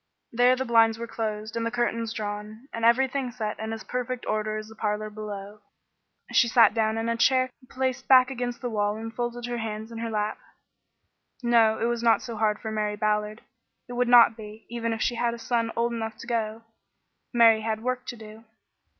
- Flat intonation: Yes, narrow, 1.9 semitones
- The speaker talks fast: Yes, fast, 210 wpm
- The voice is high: Yes, high, 230 Hz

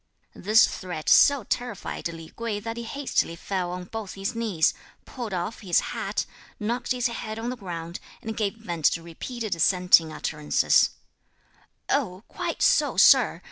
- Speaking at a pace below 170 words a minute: Yes, average, 155 wpm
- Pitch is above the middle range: Yes, high, 205 Hz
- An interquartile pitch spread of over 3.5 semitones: Yes, average, 4.9 semitones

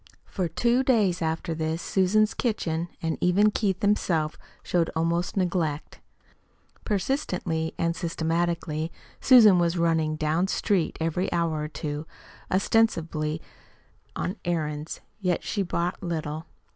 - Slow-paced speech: Yes, slow, 120 wpm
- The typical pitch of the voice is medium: Yes, medium, 170 Hz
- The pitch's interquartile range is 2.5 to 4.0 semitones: Yes, average, 2.9 semitones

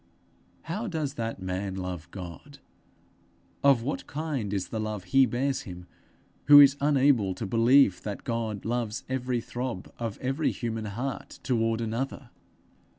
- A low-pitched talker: Yes, low, 115 Hz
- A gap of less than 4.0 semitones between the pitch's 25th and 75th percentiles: No, average, 4.8 semitones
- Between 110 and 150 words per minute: Yes, average, 145 wpm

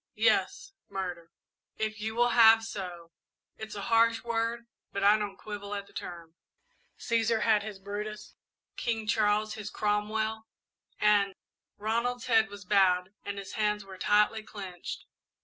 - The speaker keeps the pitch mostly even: Yes, narrow, 1.9 semitones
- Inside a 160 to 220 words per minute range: No, average, 150 wpm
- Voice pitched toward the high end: Yes, high, 210 Hz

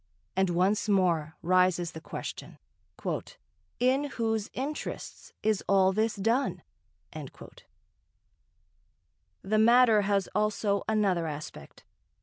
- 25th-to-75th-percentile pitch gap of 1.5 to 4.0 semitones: Yes, average, 3.2 semitones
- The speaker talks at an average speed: No, slow, 95 wpm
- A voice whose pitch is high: Yes, high, 200 Hz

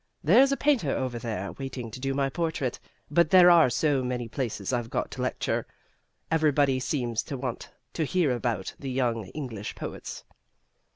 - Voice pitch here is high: No, low, 135 Hz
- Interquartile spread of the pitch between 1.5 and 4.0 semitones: No, average, 4.4 semitones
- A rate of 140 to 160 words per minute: No, average, 170 wpm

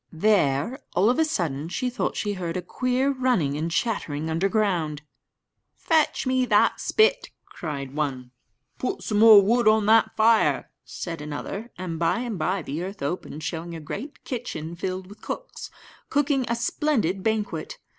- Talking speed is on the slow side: No, average, 165 wpm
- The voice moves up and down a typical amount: No, wide, 6.8 semitones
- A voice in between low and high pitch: No, high, 195 Hz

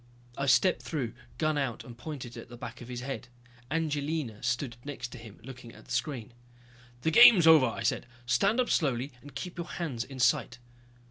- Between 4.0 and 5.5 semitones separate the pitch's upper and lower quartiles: Yes, average, 4.5 semitones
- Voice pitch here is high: No, low, 135 Hz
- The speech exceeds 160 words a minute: Yes, average, 200 wpm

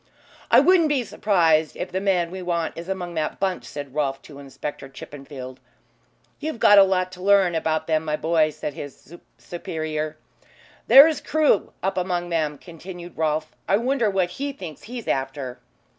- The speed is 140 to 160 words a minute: No, average, 170 wpm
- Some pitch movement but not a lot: Yes, average, 4.0 semitones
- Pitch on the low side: No, medium, 170 Hz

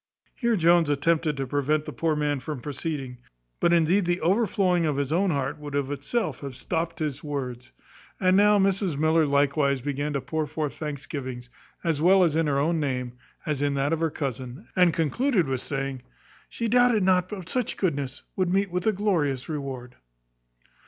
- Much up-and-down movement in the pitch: No, average, 4.3 semitones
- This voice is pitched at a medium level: Yes, medium, 155 Hz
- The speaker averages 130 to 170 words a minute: No, average, 180 wpm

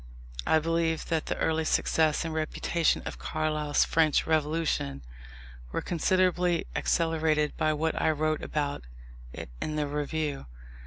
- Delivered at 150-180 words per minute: No, slow, 135 wpm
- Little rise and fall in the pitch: Yes, narrow, 1.3 semitones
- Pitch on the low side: No, medium, 155 Hz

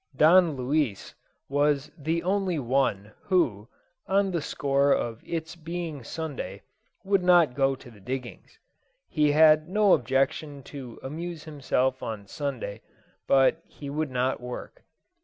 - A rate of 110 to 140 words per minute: Yes, slow, 135 wpm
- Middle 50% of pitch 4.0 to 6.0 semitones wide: Yes, average, 4.3 semitones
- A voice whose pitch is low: No, medium, 145 Hz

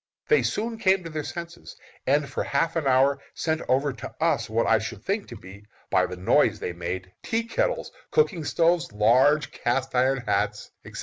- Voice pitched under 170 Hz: Yes, medium, 140 Hz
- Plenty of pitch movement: Yes, wide, 6.6 semitones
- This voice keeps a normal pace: Yes, average, 190 wpm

